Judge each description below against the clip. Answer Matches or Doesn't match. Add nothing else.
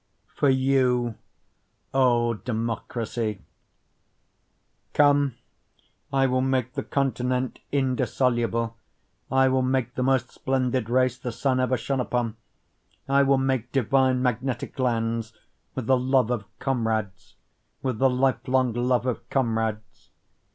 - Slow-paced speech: Matches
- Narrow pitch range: Matches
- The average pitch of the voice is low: Matches